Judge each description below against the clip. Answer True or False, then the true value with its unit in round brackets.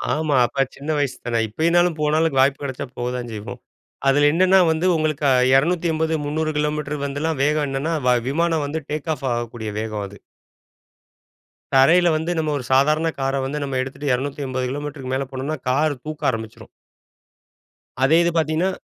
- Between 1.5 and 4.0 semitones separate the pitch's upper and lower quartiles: True (3.0 semitones)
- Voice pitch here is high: False (145 Hz)